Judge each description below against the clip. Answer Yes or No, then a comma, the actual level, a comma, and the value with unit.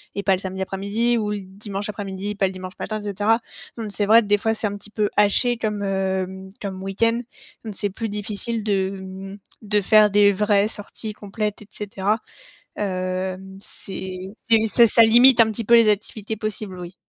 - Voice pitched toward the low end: No, high, 205 Hz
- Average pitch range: No, narrow, 2.1 semitones